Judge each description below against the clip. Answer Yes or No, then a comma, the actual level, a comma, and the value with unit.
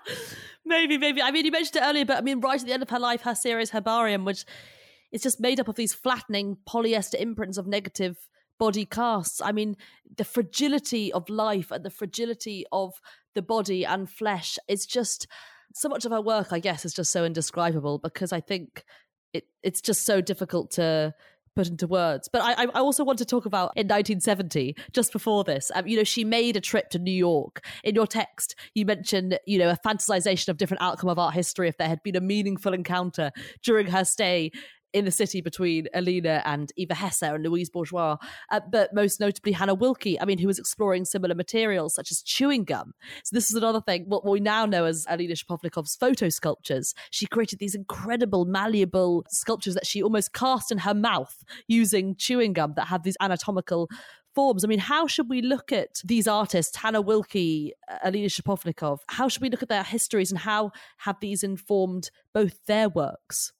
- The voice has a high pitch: Yes, high, 200 Hz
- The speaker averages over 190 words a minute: Yes, average, 200 wpm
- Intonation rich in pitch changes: No, average, 4.0 semitones